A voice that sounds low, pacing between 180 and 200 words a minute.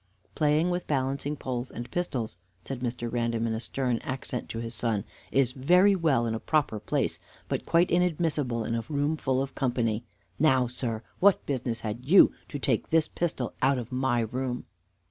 Yes: low, 130 Hz; average, 185 wpm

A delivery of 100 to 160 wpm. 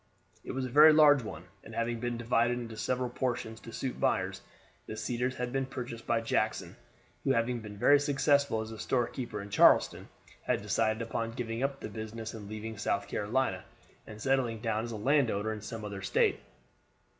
No: average, 190 wpm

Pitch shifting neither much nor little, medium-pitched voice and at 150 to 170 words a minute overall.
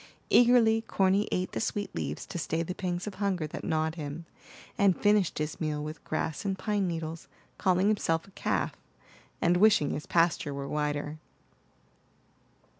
Yes: average, 4.2 semitones; medium, 175 Hz; average, 160 wpm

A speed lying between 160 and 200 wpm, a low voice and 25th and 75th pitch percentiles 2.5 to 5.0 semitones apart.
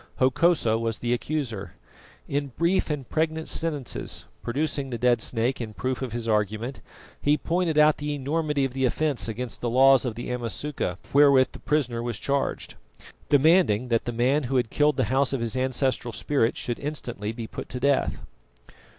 Yes: average, 175 wpm; low, 130 Hz; average, 3.8 semitones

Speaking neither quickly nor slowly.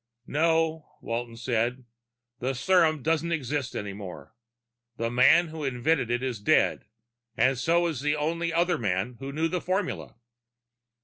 Yes: average, 145 wpm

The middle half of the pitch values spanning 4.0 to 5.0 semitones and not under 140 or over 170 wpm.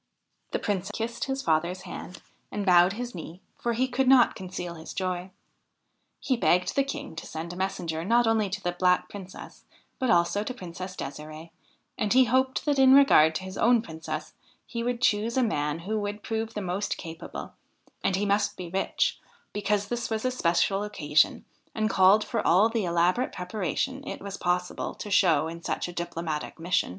No: average, 4.7 semitones; average, 190 wpm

